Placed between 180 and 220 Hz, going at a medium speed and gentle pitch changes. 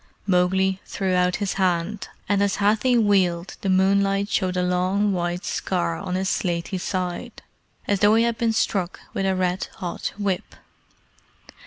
Yes: high, 190 Hz; average, 160 wpm; narrow, 2.0 semitones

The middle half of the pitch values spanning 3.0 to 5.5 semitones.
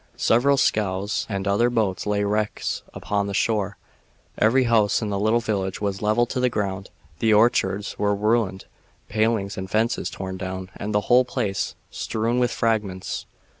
No: narrow, 2.6 semitones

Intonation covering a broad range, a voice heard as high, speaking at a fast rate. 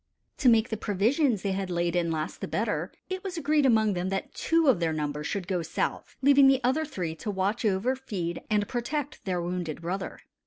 Yes: wide, 7.0 semitones; high, 205 Hz; fast, 210 wpm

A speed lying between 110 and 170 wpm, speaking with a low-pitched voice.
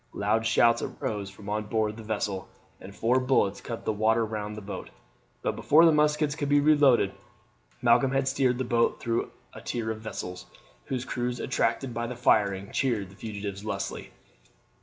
No: average, 180 wpm; low, 115 Hz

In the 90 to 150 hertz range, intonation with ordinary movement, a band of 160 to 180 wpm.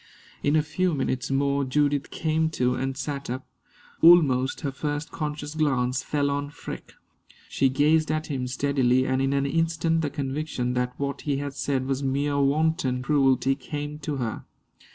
No: medium, 140 Hz; narrow, 2.3 semitones; average, 170 wpm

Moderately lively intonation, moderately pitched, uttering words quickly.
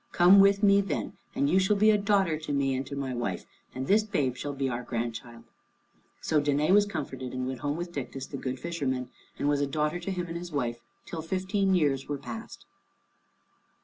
No: wide, 6.2 semitones; medium, 145 Hz; fast, 215 wpm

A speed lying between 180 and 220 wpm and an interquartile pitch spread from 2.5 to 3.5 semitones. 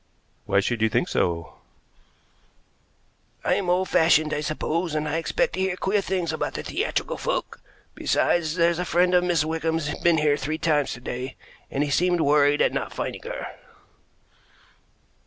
No: average, 160 wpm; average, 3.2 semitones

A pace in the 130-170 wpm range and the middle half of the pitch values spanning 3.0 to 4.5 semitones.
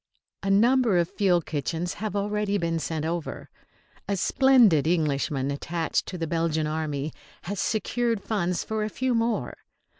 No: average, 150 wpm; average, 5.0 semitones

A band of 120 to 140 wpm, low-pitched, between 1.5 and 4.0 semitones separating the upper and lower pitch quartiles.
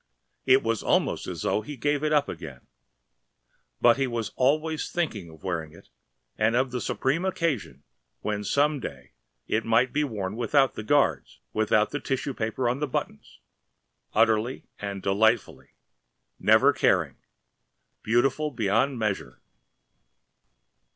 No: slow, 135 wpm; low, 120 Hz; average, 4.8 semitones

